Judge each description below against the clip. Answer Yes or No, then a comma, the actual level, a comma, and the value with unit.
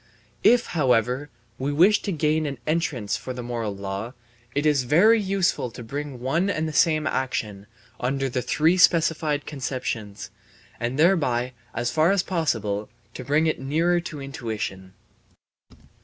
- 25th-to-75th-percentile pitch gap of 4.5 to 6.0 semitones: Yes, average, 5.0 semitones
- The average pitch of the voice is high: No, medium, 140 Hz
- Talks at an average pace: Yes, average, 150 wpm